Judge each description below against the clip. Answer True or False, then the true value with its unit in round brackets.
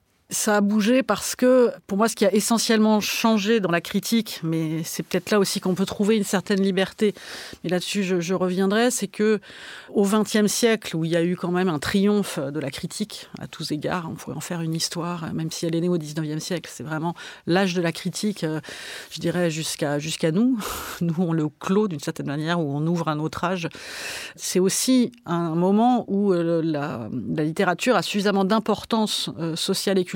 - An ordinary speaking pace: True (205 wpm)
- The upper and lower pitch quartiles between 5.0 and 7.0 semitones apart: False (4.0 semitones)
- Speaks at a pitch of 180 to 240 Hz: True (185 Hz)